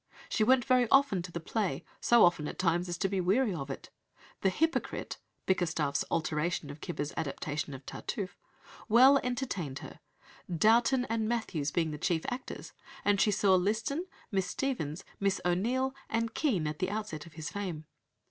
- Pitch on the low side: No, high, 190 Hz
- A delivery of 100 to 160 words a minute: No, average, 170 wpm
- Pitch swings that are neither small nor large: No, wide, 6.1 semitones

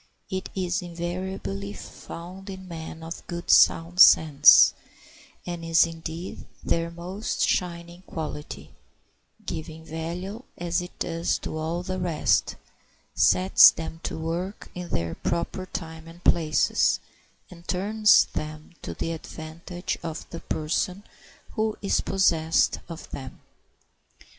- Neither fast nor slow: No, slow, 125 wpm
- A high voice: No, medium, 170 Hz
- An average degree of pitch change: No, narrow, 2.0 semitones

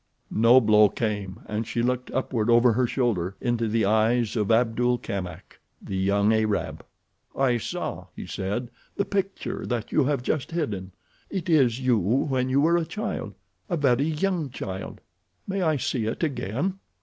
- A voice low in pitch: Yes, low, 120 Hz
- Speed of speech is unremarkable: Yes, average, 160 wpm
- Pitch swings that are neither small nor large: Yes, average, 4.6 semitones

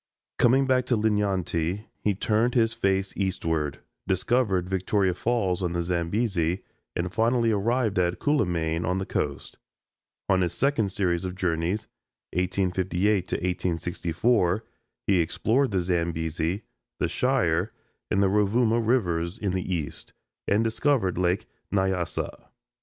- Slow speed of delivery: Yes, slow, 125 wpm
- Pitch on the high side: No, very low, 95 Hz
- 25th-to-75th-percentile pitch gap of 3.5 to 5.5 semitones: Yes, average, 4.0 semitones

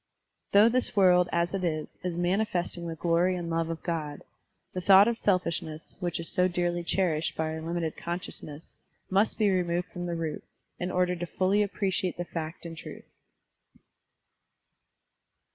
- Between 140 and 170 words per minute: Yes, average, 165 wpm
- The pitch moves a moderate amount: No, narrow, 1.9 semitones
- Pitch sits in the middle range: Yes, medium, 175 Hz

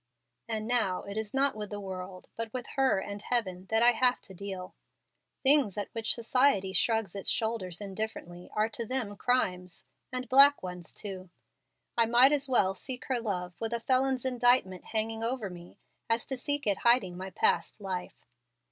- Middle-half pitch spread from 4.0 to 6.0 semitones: Yes, average, 4.6 semitones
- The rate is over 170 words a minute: Yes, average, 180 wpm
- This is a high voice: Yes, high, 220 Hz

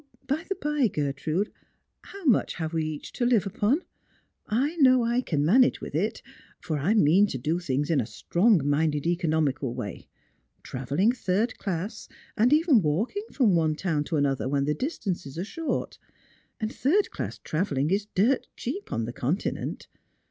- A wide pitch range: Yes, wide, 8.2 semitones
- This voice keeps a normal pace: Yes, average, 175 wpm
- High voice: No, medium, 180 Hz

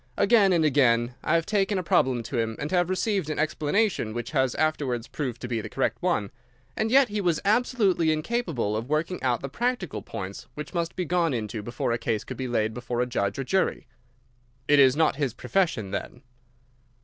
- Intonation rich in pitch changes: Yes, wide, 7.3 semitones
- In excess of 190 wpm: Yes, fast, 205 wpm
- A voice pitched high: No, medium, 145 Hz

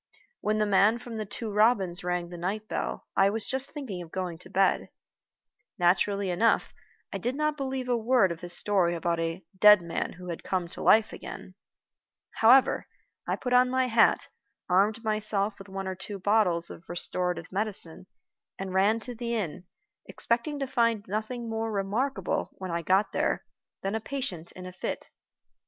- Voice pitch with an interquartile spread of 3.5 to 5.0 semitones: Yes, average, 4.1 semitones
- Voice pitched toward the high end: Yes, high, 205 Hz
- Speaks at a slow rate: No, average, 180 wpm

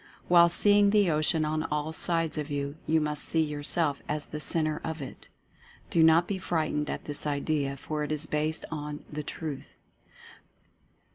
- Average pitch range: No, narrow, 1.5 semitones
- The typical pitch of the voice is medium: Yes, medium, 155 Hz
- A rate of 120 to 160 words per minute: No, average, 170 wpm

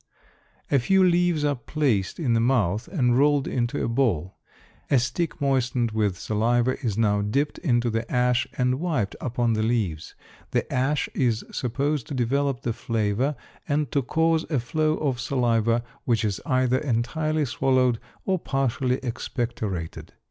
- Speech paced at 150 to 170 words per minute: Yes, average, 155 wpm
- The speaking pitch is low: Yes, low, 125 Hz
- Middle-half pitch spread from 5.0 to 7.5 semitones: No, average, 3.7 semitones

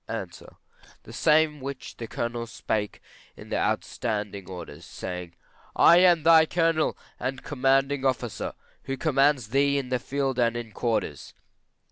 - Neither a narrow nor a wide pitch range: Yes, average, 3.8 semitones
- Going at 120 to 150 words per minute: Yes, average, 140 wpm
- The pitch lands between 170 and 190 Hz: No, low, 130 Hz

